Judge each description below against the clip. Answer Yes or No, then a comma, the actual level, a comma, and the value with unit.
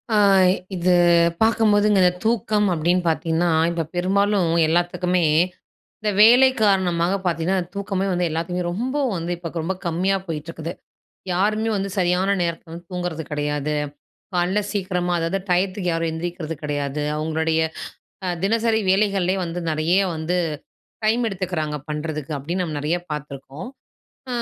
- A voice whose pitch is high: No, medium, 175 Hz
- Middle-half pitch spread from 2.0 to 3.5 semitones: Yes, average, 3.2 semitones